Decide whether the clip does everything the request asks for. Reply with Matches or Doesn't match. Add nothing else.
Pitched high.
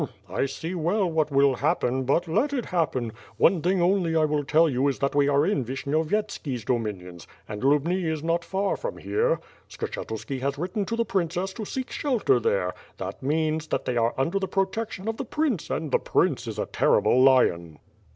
Doesn't match